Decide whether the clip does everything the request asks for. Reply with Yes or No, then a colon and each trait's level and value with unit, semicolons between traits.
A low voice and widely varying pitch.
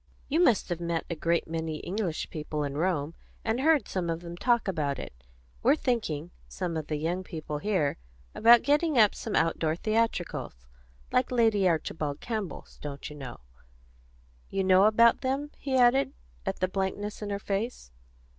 No: medium, 185 Hz; wide, 6.2 semitones